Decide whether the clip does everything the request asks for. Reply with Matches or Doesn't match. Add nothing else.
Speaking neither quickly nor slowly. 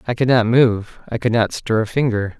Doesn't match